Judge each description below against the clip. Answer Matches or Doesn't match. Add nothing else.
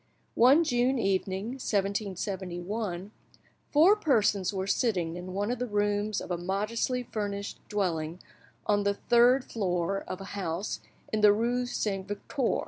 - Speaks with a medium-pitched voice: Doesn't match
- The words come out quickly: Doesn't match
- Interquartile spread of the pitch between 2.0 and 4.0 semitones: Matches